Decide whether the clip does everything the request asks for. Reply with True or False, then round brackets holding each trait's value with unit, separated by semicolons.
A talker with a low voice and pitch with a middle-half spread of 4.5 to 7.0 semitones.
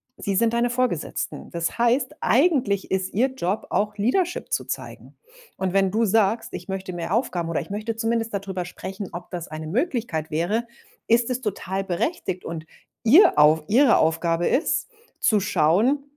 False (200 Hz; 5.1 semitones)